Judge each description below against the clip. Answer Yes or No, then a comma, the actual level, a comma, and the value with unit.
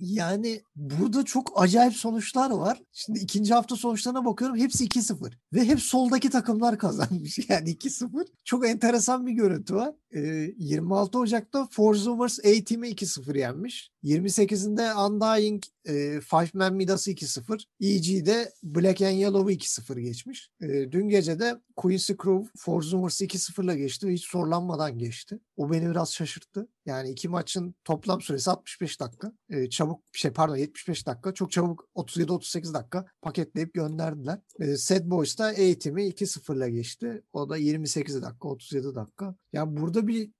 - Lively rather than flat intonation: Yes, wide, 5.7 semitones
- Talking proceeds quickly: Yes, fast, 145 wpm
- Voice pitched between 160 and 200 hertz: Yes, high, 190 Hz